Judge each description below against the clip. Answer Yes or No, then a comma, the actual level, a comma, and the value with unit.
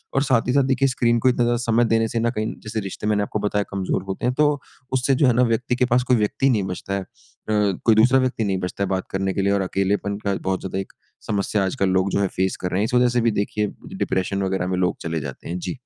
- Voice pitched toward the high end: No, low, 105 Hz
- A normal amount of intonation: Yes, average, 4.2 semitones